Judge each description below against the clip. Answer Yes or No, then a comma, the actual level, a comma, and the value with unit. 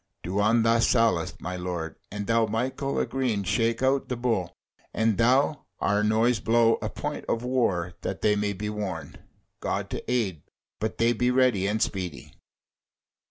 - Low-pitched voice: Yes, low, 110 Hz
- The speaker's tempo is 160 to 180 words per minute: Yes, average, 170 wpm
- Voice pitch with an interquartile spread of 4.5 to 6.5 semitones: No, average, 3.2 semitones